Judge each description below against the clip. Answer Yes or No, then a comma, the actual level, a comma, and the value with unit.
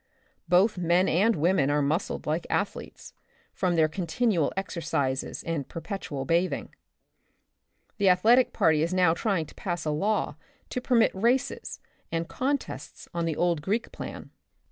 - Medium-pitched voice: Yes, medium, 175 Hz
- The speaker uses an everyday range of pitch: Yes, average, 4.0 semitones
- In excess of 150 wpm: No, average, 145 wpm